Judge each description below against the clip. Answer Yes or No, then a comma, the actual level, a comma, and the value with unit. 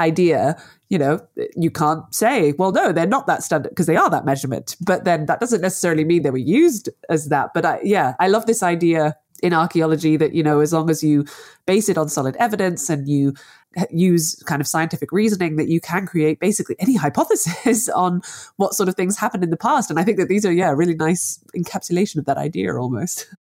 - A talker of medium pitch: Yes, medium, 170 Hz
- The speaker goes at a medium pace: No, fast, 220 wpm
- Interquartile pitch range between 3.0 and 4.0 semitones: Yes, average, 3.4 semitones